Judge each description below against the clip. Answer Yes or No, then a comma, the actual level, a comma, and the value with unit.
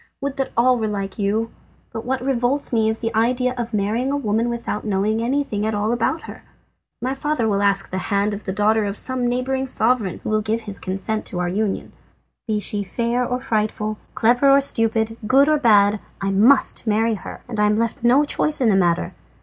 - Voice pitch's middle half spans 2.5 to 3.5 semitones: Yes, average, 3.2 semitones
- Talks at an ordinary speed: No, fast, 210 wpm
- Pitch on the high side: Yes, high, 225 Hz